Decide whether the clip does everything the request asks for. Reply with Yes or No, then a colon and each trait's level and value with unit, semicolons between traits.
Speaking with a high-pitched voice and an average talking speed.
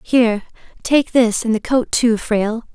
Yes: high, 230 Hz; average, 175 wpm